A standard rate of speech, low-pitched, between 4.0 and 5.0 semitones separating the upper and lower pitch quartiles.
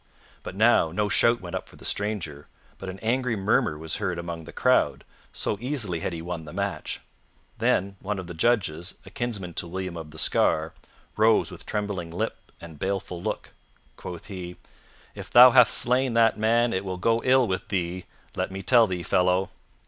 Yes: average, 190 wpm; very low, 95 Hz; average, 4.6 semitones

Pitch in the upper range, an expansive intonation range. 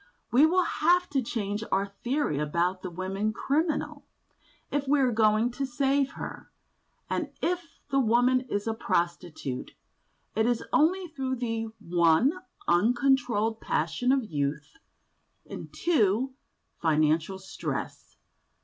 Yes: high, 225 Hz; wide, 6.6 semitones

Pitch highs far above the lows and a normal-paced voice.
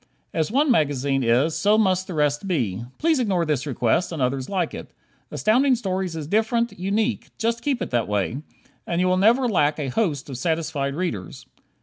Yes: wide, 7.6 semitones; average, 190 wpm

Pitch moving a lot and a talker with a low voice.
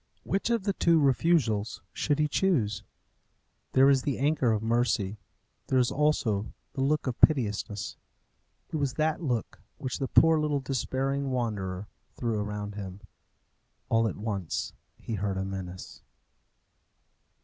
Yes: wide, 5.8 semitones; low, 125 Hz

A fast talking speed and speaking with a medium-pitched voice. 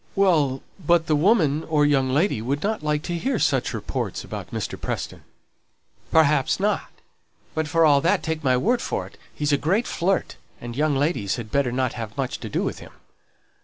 No: average, 195 wpm; medium, 150 Hz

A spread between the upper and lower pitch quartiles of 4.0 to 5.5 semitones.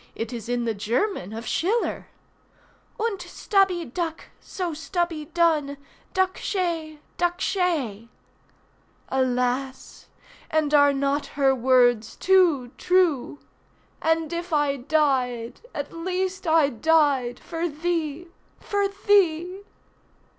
Yes: average, 5.2 semitones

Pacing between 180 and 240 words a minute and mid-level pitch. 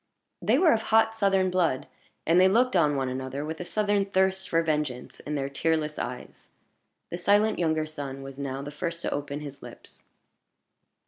Yes: average, 185 wpm; medium, 160 Hz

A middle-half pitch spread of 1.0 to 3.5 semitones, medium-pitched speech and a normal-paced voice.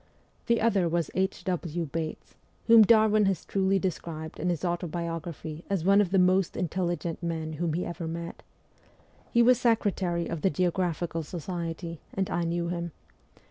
Yes: narrow, 2.4 semitones; medium, 175 Hz; average, 160 wpm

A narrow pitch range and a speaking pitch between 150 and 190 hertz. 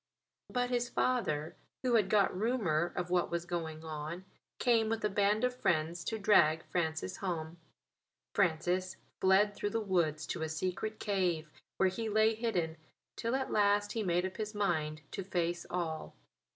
No: average, 4.5 semitones; medium, 185 Hz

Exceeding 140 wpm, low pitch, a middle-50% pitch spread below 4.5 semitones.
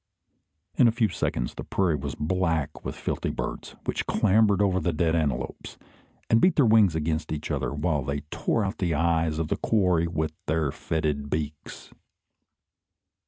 Yes: average, 165 wpm; very low, 80 Hz; average, 4.0 semitones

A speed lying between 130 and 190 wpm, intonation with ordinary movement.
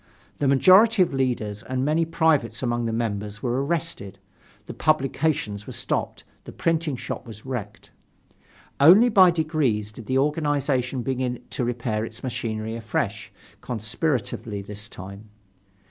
No: slow, 135 wpm; wide, 5.9 semitones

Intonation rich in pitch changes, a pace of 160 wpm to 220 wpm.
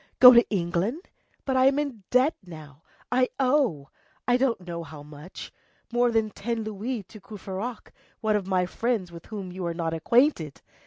Yes: wide, 6.2 semitones; average, 175 wpm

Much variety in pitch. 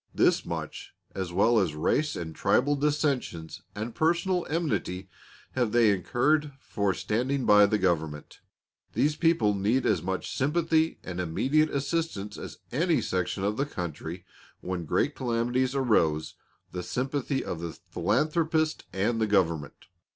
Yes: wide, 8.0 semitones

